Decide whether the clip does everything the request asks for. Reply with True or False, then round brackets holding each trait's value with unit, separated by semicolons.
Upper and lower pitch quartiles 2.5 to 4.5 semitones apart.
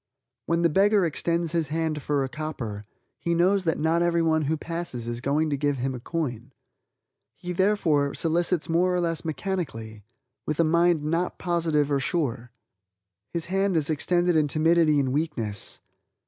True (3.3 semitones)